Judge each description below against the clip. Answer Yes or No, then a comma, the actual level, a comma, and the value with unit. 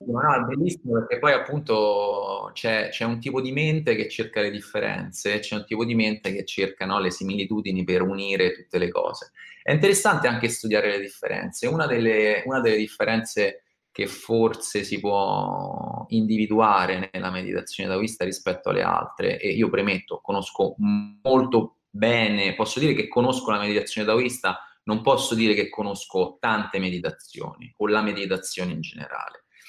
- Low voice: Yes, low, 115 Hz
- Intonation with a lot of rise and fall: Yes, wide, 7.0 semitones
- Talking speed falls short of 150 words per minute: No, average, 160 wpm